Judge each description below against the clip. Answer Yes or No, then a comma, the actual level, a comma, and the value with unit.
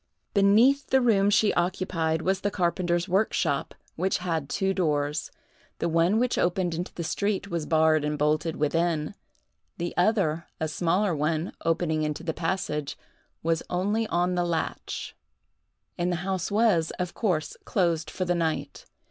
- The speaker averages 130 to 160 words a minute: Yes, average, 155 wpm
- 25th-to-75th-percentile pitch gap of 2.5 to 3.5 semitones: Yes, average, 3.1 semitones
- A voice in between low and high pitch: Yes, medium, 175 Hz